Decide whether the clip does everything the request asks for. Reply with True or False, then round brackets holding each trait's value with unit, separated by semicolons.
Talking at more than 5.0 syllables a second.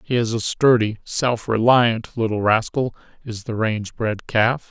False (4.2 syllables/s)